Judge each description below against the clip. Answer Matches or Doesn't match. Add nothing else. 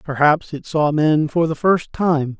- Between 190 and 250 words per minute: Matches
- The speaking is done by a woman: Doesn't match